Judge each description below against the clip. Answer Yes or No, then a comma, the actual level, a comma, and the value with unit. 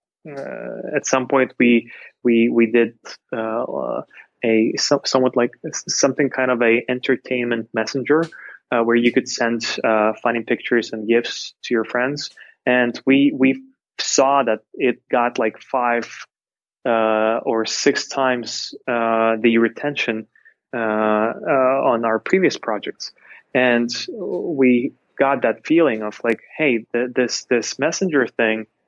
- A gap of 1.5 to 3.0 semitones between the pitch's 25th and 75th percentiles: Yes, narrow, 2.5 semitones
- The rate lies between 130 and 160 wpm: Yes, slow, 135 wpm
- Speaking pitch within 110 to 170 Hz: Yes, low, 120 Hz